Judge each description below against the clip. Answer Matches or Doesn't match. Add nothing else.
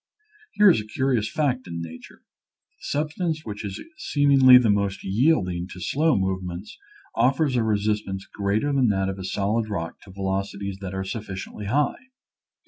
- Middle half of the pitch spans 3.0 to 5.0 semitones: Doesn't match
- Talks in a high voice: Doesn't match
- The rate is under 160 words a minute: Doesn't match